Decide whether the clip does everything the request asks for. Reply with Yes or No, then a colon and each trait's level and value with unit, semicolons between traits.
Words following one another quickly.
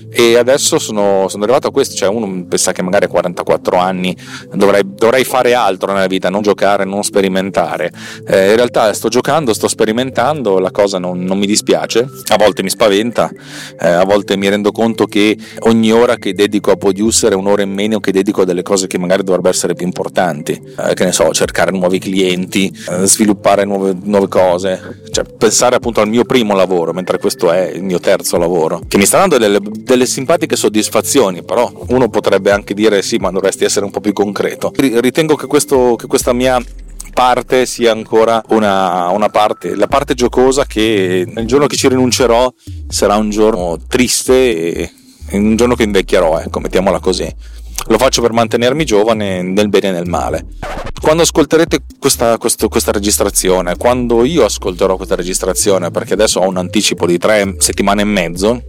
Yes: fast, 185 wpm